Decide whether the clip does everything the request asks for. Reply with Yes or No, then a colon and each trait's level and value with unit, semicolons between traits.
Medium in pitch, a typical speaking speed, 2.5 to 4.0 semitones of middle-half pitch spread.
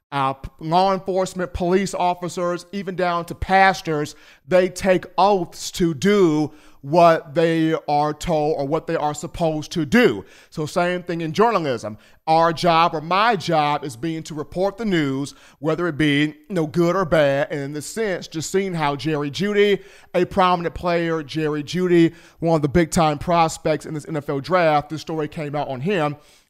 Yes: medium, 165 Hz; average, 180 wpm; average, 3.1 semitones